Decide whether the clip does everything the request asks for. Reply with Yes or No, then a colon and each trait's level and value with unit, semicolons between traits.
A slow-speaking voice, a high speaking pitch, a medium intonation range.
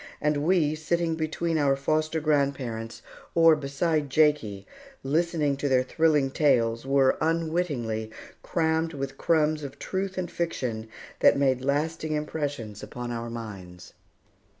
No: slow, 125 wpm; medium, 145 Hz; average, 3.8 semitones